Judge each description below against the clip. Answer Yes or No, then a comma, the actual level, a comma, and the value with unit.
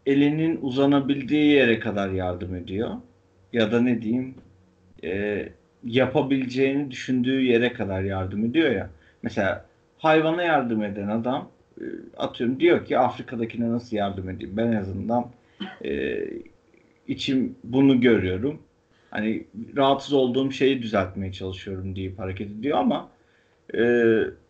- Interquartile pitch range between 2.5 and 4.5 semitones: No, average, 5.2 semitones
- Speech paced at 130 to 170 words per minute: No, average, 120 wpm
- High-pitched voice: No, low, 120 Hz